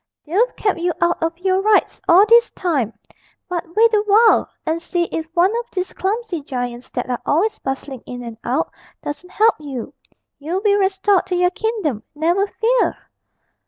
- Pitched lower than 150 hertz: No, very high, 360 Hz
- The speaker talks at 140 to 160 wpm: No, average, 175 wpm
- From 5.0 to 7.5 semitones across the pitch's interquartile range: Yes, wide, 5.5 semitones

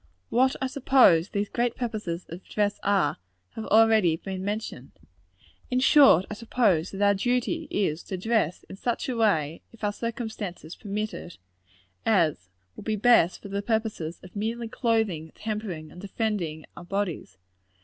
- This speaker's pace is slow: No, average, 160 wpm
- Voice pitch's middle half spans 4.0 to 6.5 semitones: Yes, average, 4.5 semitones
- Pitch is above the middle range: Yes, high, 205 Hz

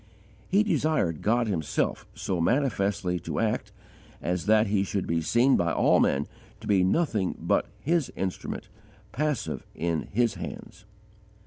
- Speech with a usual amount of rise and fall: No, wide, 6.3 semitones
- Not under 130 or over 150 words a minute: Yes, average, 140 wpm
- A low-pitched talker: Yes, low, 100 Hz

